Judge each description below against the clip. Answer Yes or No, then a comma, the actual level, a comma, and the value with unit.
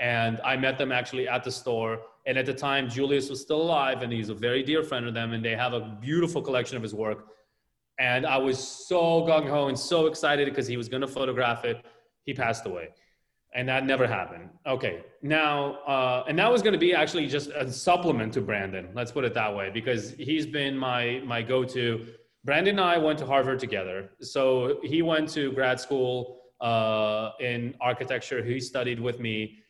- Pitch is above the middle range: No, low, 130 Hz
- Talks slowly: No, fast, 205 wpm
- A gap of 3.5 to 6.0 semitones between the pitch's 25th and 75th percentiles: No, average, 3.0 semitones